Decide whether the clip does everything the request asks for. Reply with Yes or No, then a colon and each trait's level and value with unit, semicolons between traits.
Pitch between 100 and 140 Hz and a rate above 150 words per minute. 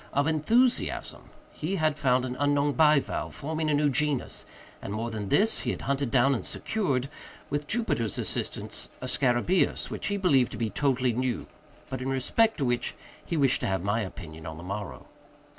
Yes: low, 135 Hz; average, 185 wpm